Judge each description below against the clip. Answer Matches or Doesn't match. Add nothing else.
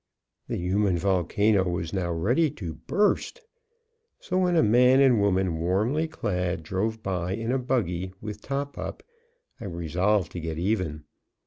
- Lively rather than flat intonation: Matches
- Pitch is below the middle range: Matches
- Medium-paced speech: Matches